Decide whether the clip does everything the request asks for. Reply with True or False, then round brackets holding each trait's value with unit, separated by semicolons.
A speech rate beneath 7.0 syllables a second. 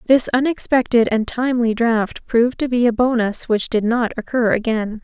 True (5.0 syllables/s)